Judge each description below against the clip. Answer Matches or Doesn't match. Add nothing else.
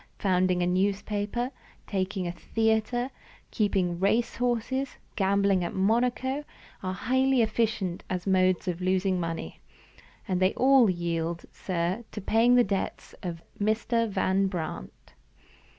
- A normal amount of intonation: Matches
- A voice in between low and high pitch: Doesn't match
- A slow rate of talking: Matches